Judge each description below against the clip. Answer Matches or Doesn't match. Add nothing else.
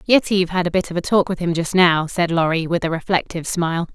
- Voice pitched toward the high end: Doesn't match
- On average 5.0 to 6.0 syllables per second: Doesn't match